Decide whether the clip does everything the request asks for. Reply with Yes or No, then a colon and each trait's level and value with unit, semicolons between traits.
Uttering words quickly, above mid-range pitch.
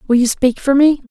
Yes: fast, 270 wpm; very high, 265 Hz